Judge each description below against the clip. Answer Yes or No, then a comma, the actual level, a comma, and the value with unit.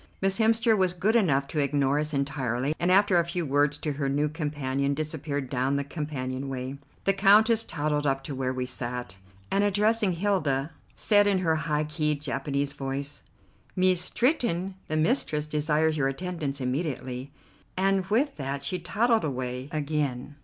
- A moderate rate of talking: Yes, average, 165 wpm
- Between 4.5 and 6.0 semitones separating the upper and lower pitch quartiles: Yes, average, 5.0 semitones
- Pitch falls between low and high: Yes, medium, 150 Hz